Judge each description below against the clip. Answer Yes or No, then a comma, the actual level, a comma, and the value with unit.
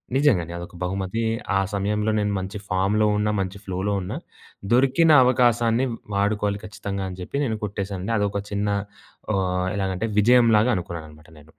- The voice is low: Yes, low, 100 Hz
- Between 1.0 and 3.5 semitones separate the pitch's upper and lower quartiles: Yes, average, 2.8 semitones